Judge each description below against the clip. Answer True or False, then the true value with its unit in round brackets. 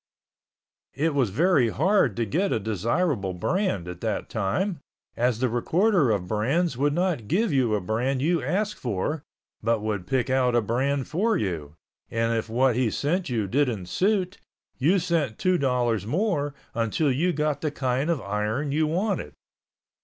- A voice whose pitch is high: False (130 Hz)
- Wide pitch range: True (7.0 semitones)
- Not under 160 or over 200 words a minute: True (170 wpm)